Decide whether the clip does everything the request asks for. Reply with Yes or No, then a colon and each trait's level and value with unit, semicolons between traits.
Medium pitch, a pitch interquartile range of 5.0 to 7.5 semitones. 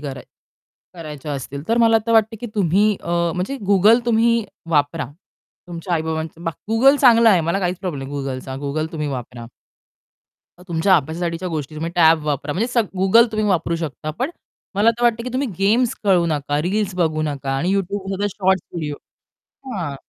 Yes: medium, 175 Hz; wide, 5.5 semitones